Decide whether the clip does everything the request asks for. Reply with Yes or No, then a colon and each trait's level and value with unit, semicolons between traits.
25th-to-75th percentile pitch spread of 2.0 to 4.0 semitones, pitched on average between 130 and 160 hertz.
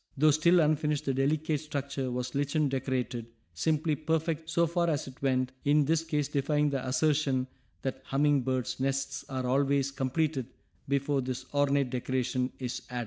Yes: average, 2.7 semitones; medium, 140 Hz